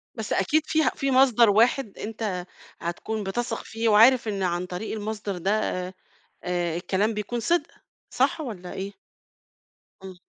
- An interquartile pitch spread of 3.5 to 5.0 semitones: Yes, average, 3.9 semitones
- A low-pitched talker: No, high, 210 Hz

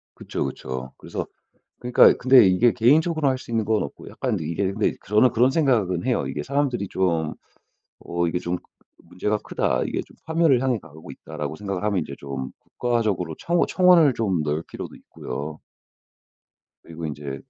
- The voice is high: No, low, 105 Hz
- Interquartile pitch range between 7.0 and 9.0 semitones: Yes, wide, 7.6 semitones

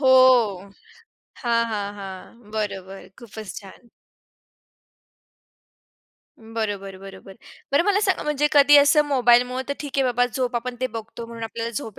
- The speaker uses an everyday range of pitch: Yes, average, 4.2 semitones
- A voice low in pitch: No, high, 235 Hz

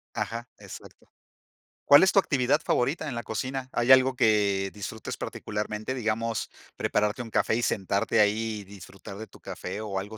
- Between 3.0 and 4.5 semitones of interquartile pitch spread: Yes, average, 3.4 semitones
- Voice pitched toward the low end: Yes, low, 110 Hz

